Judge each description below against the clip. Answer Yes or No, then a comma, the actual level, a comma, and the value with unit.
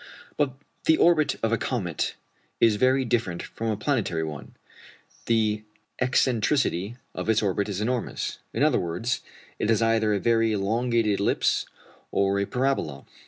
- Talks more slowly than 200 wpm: Yes, average, 150 wpm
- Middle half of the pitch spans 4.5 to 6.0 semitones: No, average, 3.7 semitones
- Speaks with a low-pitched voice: Yes, low, 115 Hz